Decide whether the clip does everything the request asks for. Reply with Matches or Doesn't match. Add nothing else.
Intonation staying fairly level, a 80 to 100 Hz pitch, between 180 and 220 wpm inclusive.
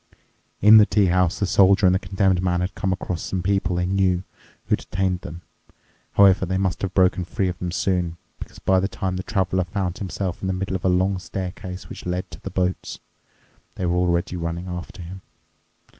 Matches